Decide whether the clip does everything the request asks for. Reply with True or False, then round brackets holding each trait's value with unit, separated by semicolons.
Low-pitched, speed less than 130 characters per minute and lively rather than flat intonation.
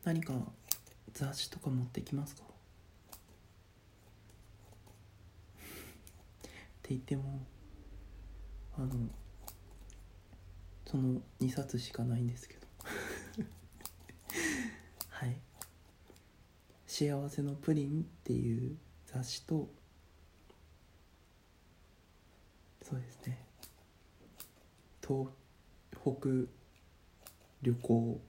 True (105 Hz; 120 characters per minute; 6.3 semitones)